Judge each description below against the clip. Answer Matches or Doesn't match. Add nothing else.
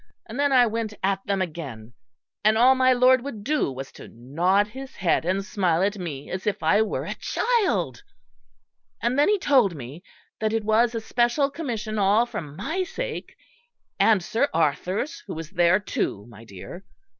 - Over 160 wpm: Matches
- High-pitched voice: Matches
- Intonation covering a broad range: Matches